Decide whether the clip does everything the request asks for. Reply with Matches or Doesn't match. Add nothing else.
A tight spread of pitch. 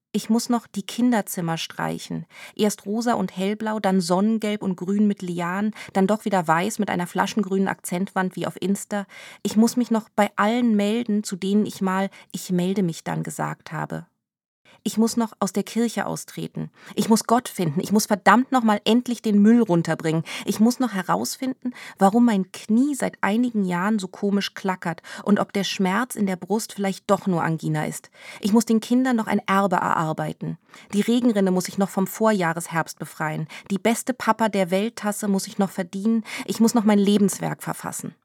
Doesn't match